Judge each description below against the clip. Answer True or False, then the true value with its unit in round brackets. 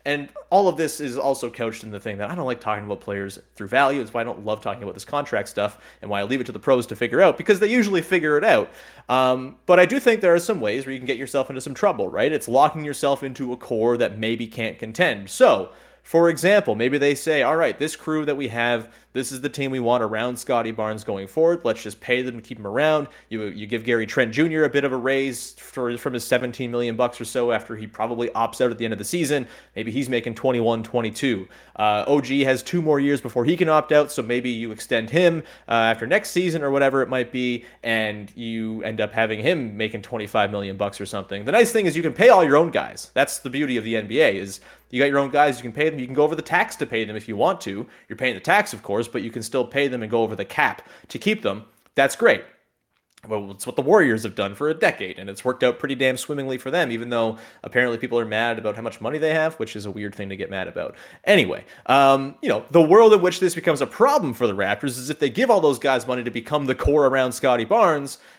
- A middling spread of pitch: True (4.4 semitones)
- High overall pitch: False (125 Hz)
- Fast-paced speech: True (270 wpm)